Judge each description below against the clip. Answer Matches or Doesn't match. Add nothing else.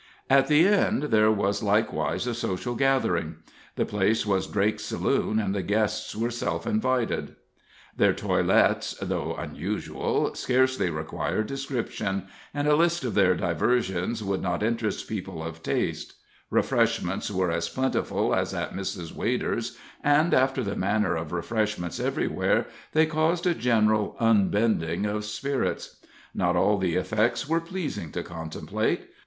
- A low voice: Matches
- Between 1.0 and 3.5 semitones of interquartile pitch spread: Doesn't match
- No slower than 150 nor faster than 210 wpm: Doesn't match